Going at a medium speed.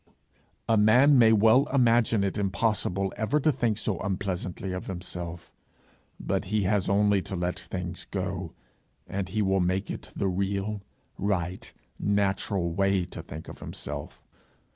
Yes: average, 145 wpm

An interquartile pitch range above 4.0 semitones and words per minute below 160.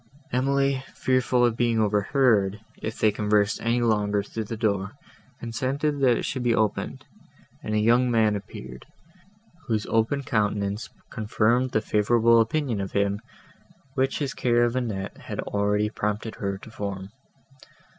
No: average, 2.9 semitones; average, 145 wpm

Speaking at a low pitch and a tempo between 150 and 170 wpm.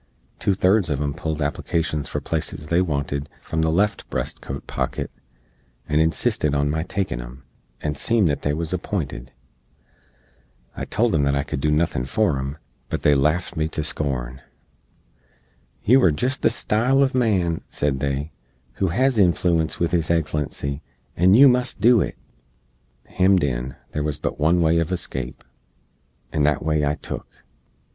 Yes: very low, 80 Hz; average, 165 wpm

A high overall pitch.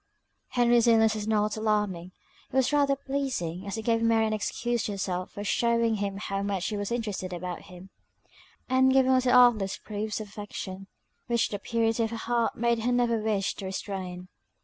Yes: high, 220 Hz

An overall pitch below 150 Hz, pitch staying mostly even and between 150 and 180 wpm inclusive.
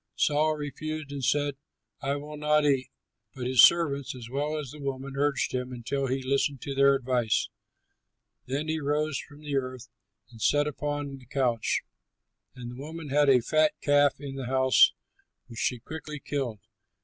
Yes: medium, 140 Hz; narrow, 2.2 semitones; average, 175 wpm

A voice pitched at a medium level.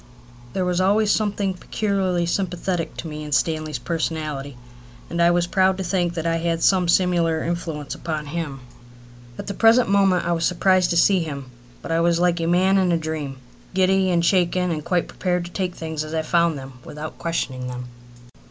Yes: medium, 170 Hz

